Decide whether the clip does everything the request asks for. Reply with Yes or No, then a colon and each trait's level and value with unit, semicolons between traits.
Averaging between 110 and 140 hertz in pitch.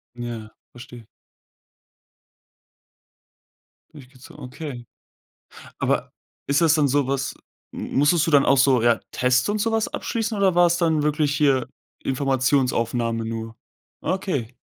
Yes: low, 135 Hz